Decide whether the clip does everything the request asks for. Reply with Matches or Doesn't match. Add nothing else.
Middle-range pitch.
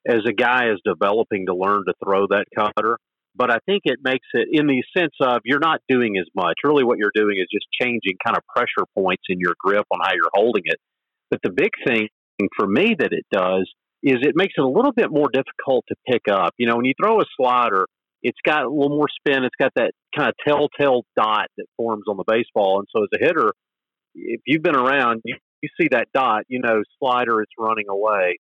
Doesn't match